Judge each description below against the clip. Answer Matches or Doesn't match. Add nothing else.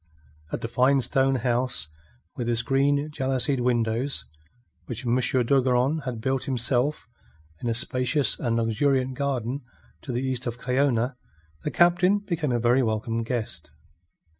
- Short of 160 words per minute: Matches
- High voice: Doesn't match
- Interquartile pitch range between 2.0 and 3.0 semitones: Matches